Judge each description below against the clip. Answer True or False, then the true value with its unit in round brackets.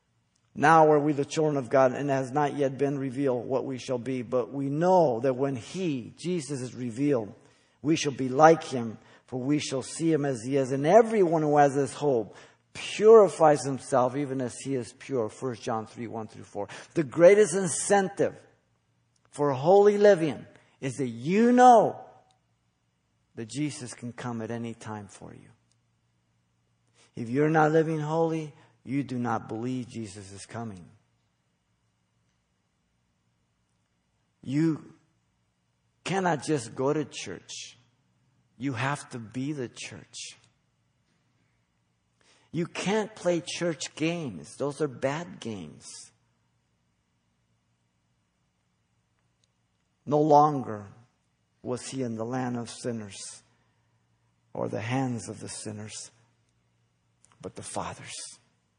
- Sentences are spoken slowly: True (130 wpm)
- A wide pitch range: False (5.0 semitones)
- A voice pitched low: True (130 Hz)